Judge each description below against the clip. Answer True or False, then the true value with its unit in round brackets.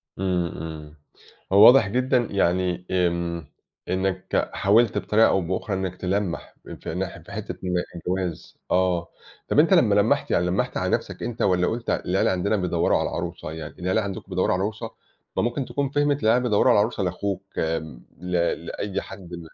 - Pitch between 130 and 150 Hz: False (95 Hz)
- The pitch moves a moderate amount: True (3.5 semitones)